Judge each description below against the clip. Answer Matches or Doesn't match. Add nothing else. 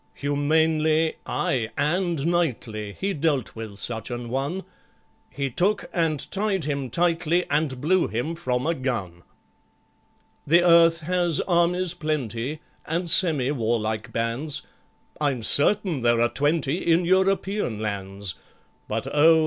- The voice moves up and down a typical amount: Doesn't match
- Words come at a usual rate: Doesn't match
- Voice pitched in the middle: Matches